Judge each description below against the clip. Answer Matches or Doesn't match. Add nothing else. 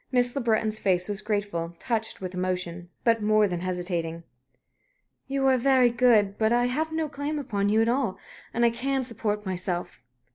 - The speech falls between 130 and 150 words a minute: Doesn't match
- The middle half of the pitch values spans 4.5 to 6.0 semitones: Matches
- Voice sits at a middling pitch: Doesn't match